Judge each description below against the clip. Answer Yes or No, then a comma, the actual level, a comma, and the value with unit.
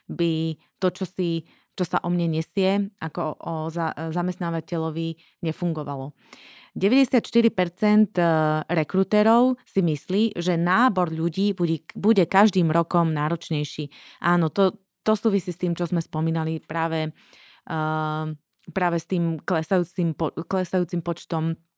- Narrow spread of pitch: No, average, 3.0 semitones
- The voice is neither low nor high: Yes, medium, 170 Hz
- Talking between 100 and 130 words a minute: Yes, average, 115 wpm